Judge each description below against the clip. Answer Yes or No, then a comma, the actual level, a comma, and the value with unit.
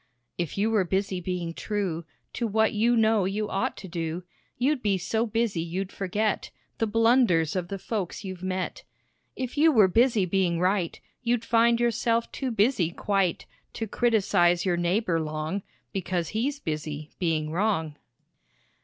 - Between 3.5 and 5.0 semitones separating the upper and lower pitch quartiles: Yes, average, 4.5 semitones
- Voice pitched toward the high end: Yes, high, 195 Hz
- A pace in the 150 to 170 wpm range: Yes, average, 155 wpm